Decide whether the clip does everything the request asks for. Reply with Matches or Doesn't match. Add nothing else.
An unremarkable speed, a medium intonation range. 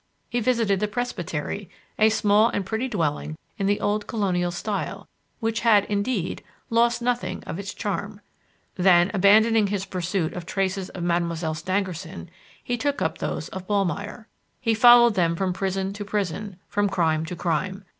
Matches